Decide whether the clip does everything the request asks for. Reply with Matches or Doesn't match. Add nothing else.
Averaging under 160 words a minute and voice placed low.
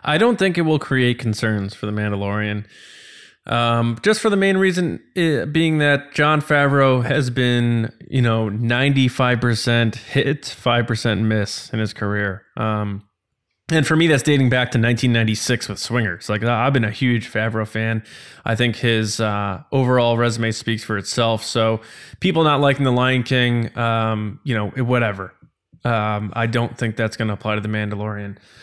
Doesn't match